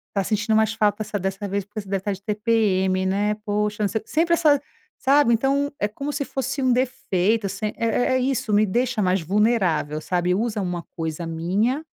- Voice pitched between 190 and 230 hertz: Yes, high, 210 Hz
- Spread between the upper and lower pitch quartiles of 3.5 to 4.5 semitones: Yes, average, 4.1 semitones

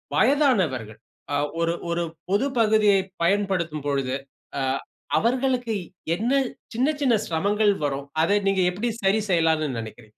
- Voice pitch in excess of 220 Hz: No, high, 190 Hz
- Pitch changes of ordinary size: No, wide, 6.3 semitones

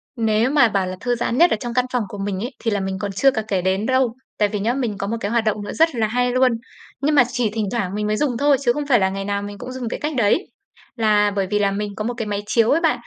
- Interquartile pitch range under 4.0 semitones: Yes, average, 3.4 semitones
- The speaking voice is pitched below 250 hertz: Yes, high, 220 Hz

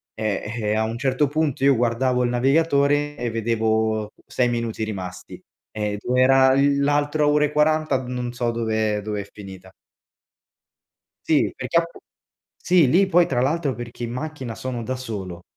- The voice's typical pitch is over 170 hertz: No, low, 125 Hz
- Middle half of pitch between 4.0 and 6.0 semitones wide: Yes, average, 4.6 semitones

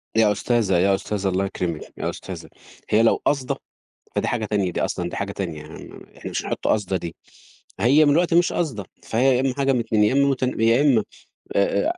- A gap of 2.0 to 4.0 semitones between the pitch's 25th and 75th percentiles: No, average, 5.3 semitones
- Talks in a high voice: No, low, 110 Hz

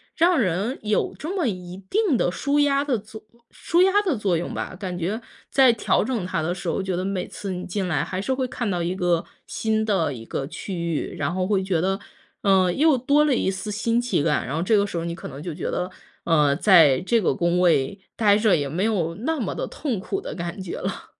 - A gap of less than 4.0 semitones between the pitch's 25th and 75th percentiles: No, average, 5.3 semitones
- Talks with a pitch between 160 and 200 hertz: Yes, high, 190 Hz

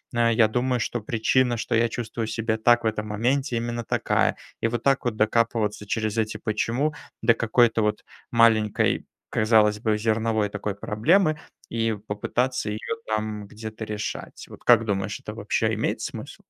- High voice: No, low, 115 Hz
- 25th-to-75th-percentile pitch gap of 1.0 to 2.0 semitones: Yes, narrow, 1.7 semitones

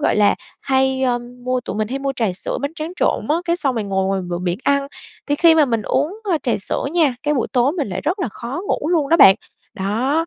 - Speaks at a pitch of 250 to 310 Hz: Yes, very high, 265 Hz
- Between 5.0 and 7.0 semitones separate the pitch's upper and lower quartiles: Yes, wide, 5.6 semitones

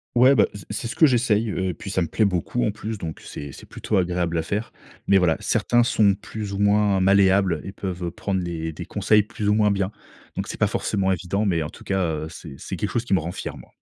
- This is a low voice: Yes, low, 100 Hz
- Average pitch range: Yes, average, 3.1 semitones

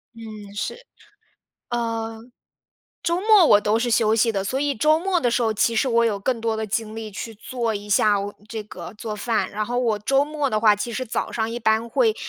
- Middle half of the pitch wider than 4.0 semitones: No, average, 2.7 semitones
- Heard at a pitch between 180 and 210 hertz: No, high, 225 Hz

